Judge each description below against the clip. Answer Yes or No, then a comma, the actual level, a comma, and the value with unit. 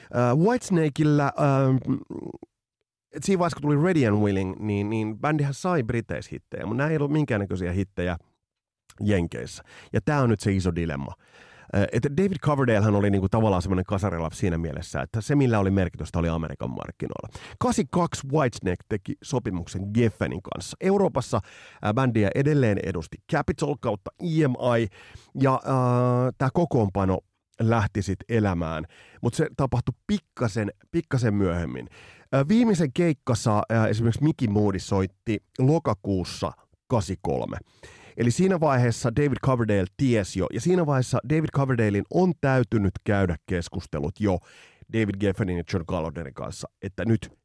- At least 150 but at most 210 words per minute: No, average, 135 wpm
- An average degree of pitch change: No, wide, 6.4 semitones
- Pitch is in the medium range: No, low, 115 Hz